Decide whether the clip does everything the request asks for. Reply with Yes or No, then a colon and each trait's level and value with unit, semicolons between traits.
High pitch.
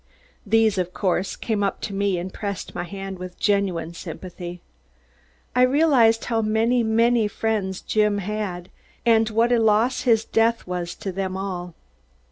Yes: high, 205 Hz